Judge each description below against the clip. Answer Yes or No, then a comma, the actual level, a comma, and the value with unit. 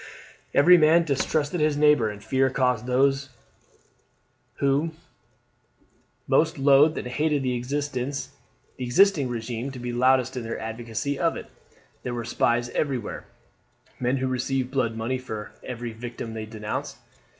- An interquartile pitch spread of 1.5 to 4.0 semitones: Yes, average, 3.0 semitones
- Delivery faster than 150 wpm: No, slow, 135 wpm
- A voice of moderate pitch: No, low, 130 Hz